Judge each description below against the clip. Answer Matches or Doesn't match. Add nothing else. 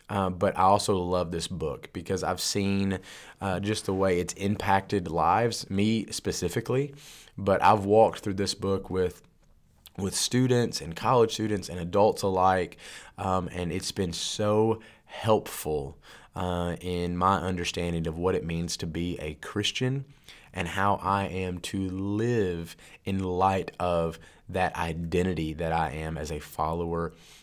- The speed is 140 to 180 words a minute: Matches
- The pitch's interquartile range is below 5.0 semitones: Matches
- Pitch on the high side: Doesn't match